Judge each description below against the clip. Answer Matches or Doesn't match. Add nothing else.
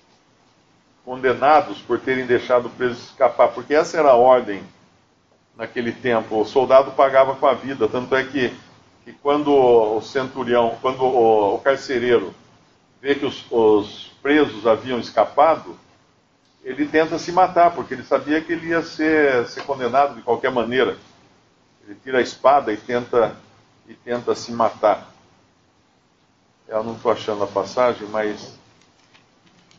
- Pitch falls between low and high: Doesn't match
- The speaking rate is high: Doesn't match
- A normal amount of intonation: Matches